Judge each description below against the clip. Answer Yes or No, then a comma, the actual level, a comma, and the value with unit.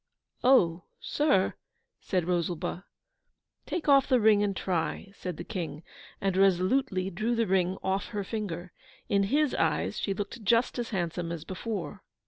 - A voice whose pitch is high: Yes, high, 195 Hz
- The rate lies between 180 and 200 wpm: No, average, 150 wpm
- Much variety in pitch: No, average, 4.2 semitones